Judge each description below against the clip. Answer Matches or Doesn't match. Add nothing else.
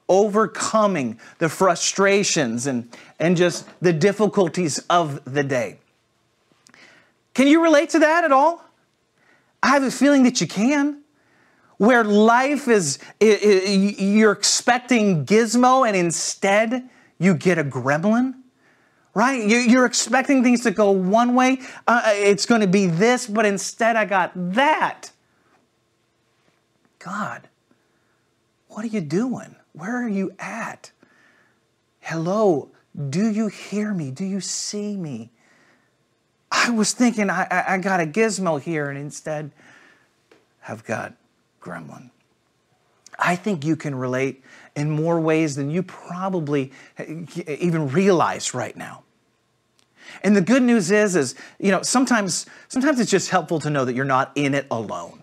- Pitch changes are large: Matches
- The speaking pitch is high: Matches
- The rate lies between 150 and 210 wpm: Doesn't match